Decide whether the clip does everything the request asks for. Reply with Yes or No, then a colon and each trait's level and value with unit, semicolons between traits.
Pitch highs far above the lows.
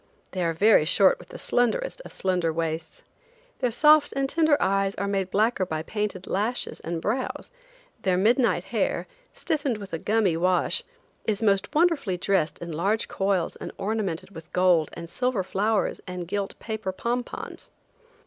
No: average, 4.5 semitones